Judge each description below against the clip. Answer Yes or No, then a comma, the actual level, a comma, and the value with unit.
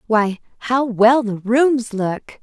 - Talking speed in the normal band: Yes, average, 150 wpm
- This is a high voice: Yes, high, 230 Hz